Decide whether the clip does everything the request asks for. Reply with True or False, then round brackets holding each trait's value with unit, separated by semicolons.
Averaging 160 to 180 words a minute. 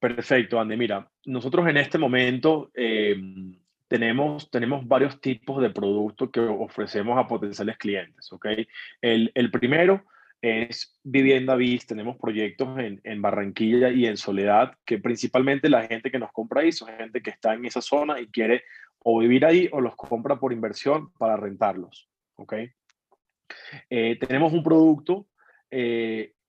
False (150 wpm)